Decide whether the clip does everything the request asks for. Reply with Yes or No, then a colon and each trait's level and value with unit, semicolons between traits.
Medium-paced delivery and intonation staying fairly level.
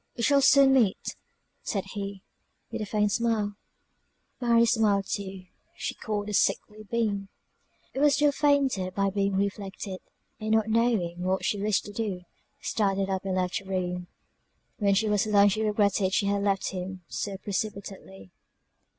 Yes: average, 160 wpm; narrow, 2.2 semitones